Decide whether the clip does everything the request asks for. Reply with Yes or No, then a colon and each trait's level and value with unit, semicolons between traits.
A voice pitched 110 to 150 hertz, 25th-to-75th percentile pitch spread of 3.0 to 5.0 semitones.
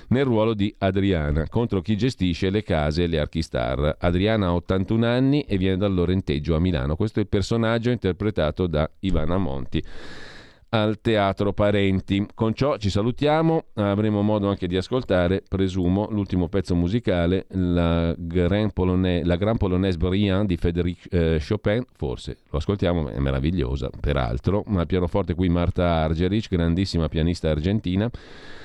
No: very low, 95 Hz; average, 3.3 semitones